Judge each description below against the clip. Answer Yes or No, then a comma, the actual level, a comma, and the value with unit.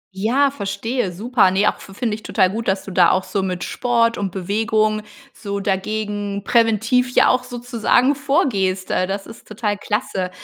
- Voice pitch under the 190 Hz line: No, high, 210 Hz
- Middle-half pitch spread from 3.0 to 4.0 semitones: Yes, average, 3.4 semitones